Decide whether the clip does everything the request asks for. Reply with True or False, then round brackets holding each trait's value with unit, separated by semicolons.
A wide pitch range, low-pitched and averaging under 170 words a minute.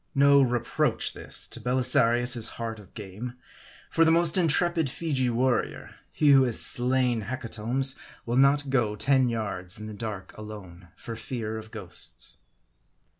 False (3.7 semitones; 120 Hz; 150 wpm)